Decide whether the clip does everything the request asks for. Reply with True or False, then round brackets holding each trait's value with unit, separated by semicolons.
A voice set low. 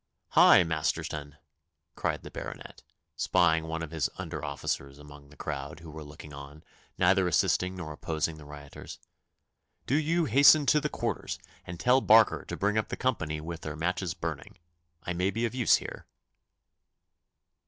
True (80 Hz)